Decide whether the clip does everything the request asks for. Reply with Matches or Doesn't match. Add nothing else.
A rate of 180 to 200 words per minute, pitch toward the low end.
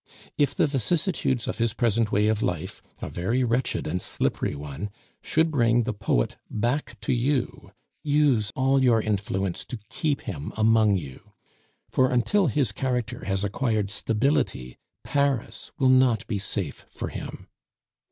Doesn't match